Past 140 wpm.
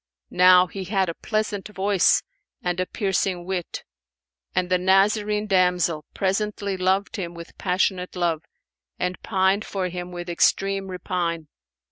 No: slow, 135 wpm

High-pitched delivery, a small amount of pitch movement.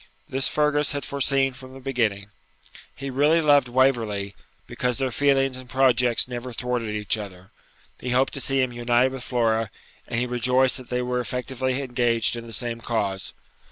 No: low, 125 Hz; narrow, 2.2 semitones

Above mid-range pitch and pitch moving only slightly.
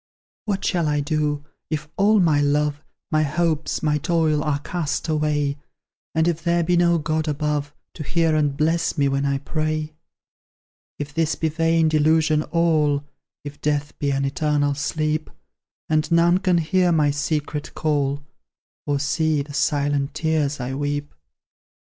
No: medium, 150 Hz; narrow, 1.8 semitones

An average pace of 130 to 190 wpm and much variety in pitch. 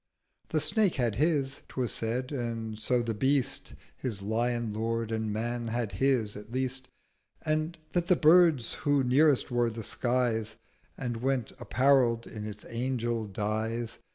No: average, 150 wpm; average, 3.1 semitones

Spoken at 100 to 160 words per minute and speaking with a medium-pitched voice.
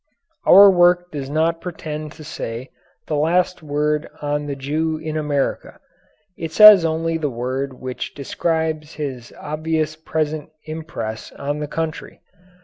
Yes: average, 140 wpm; medium, 155 Hz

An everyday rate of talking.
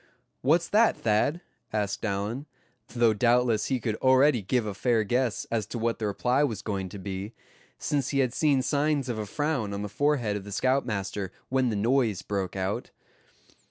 Yes: average, 185 wpm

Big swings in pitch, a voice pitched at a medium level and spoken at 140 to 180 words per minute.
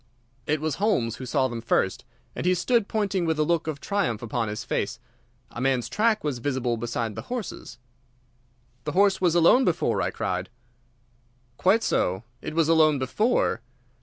Yes: wide, 7.9 semitones; medium, 150 Hz; average, 170 wpm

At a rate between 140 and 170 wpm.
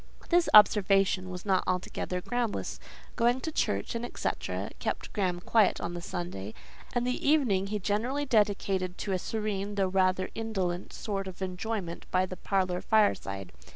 Yes: average, 155 wpm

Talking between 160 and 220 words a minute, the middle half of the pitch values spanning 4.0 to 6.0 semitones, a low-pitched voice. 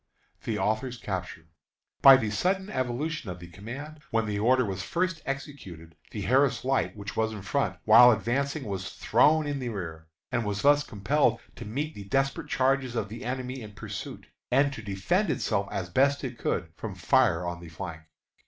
Yes: average, 185 wpm; wide, 5.5 semitones; low, 120 Hz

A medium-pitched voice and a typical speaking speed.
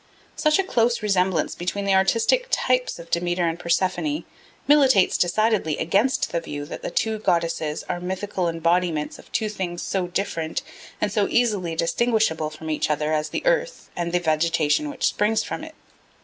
Yes: medium, 180 Hz; average, 170 wpm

